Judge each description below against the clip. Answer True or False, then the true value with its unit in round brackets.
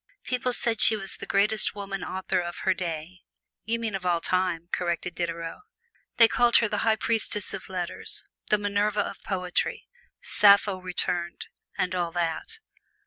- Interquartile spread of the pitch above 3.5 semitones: False (3.1 semitones)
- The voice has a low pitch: False (190 Hz)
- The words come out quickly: False (160 wpm)